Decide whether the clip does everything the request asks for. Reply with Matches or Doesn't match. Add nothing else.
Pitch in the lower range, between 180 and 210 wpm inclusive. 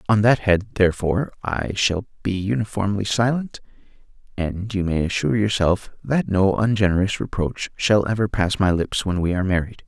Doesn't match